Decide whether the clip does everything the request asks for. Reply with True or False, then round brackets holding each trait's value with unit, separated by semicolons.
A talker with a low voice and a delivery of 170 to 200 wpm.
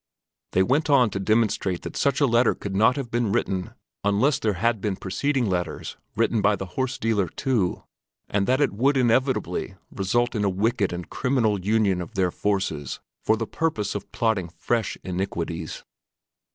True (105 Hz; 175 wpm)